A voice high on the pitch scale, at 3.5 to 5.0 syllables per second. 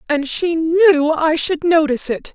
Yes: very high, 315 Hz; 4.2 syllables/s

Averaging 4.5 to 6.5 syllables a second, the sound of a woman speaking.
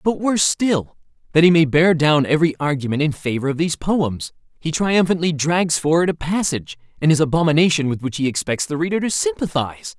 No: 5.9 syllables/s; male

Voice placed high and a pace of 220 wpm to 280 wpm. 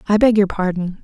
Yes: high, 200 Hz; fast, 230 wpm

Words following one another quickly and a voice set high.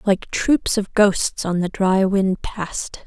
No: average, 175 wpm; high, 195 Hz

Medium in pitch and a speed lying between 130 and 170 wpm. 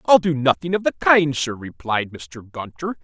No: medium, 145 Hz; average, 200 wpm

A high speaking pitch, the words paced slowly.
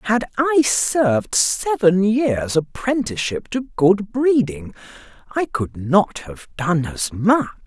Yes: high, 200 Hz; slow, 125 wpm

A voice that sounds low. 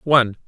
Yes: low, 125 Hz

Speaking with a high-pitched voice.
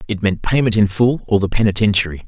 No: low, 105 Hz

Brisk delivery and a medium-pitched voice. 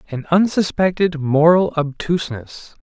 No: slow, 85 wpm; medium, 165 Hz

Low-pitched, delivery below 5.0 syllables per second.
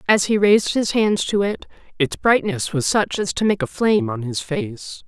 No: high, 205 Hz; 4.8 syllables/s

